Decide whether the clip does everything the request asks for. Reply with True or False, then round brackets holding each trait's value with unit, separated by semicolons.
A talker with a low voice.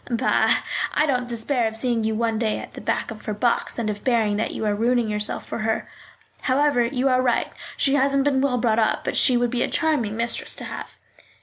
False (235 Hz)